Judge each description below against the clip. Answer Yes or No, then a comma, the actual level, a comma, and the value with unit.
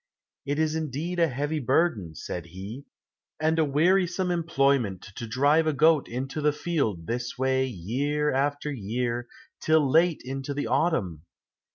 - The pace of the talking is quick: No, average, 150 wpm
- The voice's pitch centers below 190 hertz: Yes, medium, 140 Hz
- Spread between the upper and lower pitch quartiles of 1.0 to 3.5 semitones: No, average, 4.6 semitones